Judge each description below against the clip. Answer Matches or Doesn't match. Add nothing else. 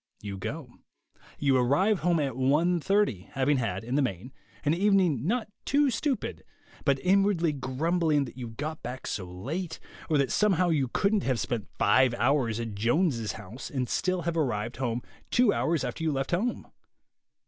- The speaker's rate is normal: Matches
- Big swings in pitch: Matches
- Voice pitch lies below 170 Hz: Matches